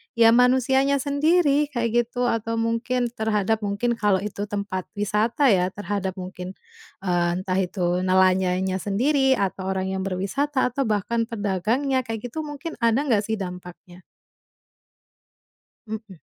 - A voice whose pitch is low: No, high, 215 Hz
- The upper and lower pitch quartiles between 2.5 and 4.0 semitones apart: No, average, 4.7 semitones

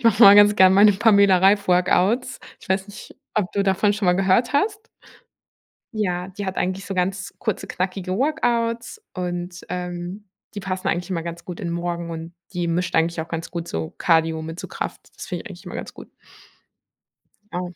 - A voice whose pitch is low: No, medium, 185 Hz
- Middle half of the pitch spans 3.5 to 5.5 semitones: No, narrow, 2.6 semitones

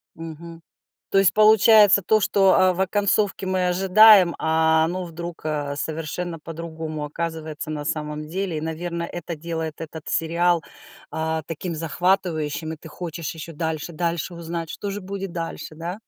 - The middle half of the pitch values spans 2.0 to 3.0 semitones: Yes, narrow, 2.5 semitones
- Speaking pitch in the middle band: Yes, medium, 165 Hz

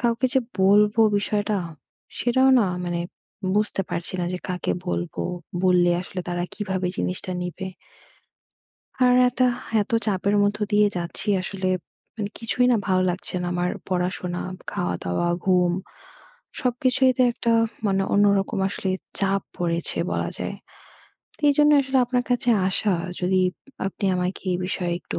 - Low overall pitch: No, high, 195 Hz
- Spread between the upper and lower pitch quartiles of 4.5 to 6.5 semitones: No, average, 3.2 semitones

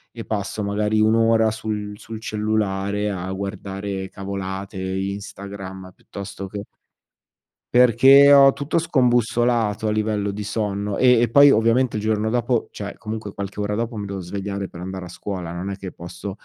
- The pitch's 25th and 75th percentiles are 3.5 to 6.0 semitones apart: No, narrow, 2.4 semitones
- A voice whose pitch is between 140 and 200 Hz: No, low, 105 Hz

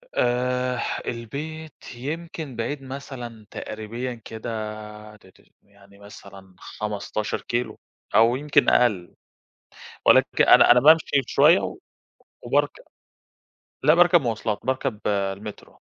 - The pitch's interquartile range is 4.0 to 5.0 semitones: Yes, average, 4.3 semitones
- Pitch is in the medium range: No, low, 120 Hz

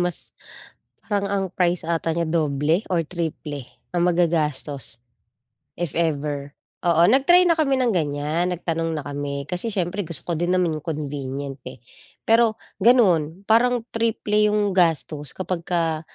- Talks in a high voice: No, medium, 170 Hz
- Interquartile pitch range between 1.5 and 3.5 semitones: No, average, 4.7 semitones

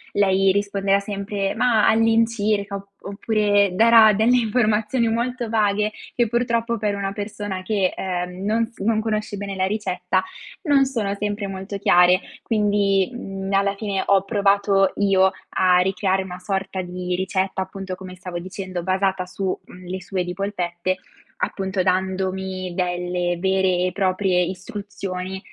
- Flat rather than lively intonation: Yes, narrow, 2.0 semitones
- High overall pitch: Yes, high, 195 Hz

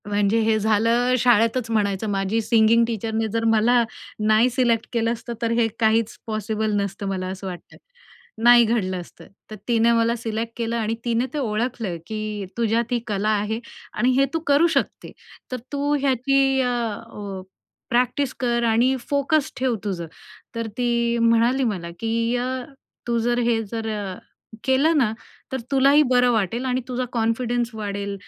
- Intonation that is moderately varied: No, narrow, 2.2 semitones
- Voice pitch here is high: Yes, high, 230 Hz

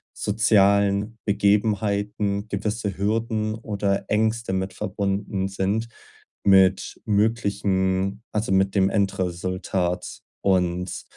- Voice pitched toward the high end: No, low, 100 Hz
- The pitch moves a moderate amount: No, narrow, 1.8 semitones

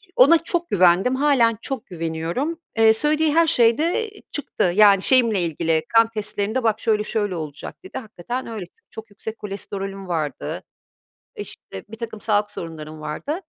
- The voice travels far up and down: Yes, wide, 6.1 semitones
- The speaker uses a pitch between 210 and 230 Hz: Yes, high, 220 Hz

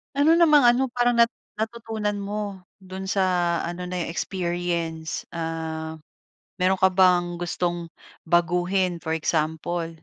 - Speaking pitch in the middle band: Yes, medium, 180 Hz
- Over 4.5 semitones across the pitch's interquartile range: No, average, 3.3 semitones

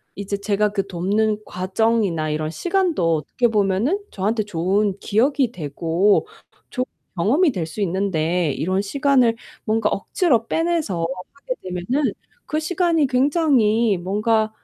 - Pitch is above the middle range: Yes, high, 210 Hz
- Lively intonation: Yes, wide, 5.8 semitones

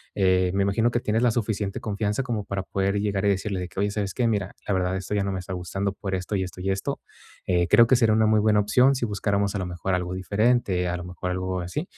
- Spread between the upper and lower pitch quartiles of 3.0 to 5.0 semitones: No, narrow, 2.6 semitones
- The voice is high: No, low, 100 Hz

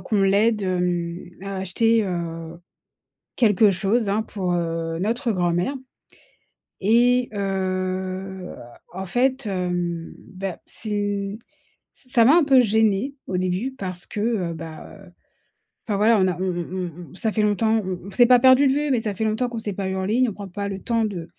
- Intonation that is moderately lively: Yes, average, 3.7 semitones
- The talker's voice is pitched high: Yes, high, 195 Hz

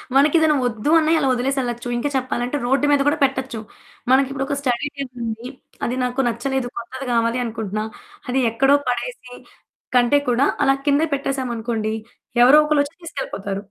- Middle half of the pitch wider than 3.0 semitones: No, average, 2.7 semitones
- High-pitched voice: Yes, very high, 260 Hz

